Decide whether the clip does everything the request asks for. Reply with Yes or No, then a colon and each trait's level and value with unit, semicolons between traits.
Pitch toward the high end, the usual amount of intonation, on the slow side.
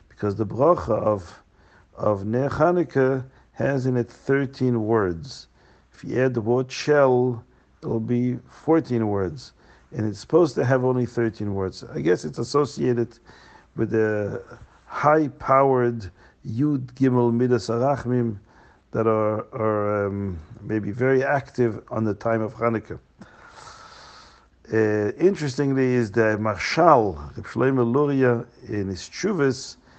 No: low, 120 Hz; average, 3.5 semitones; slow, 125 wpm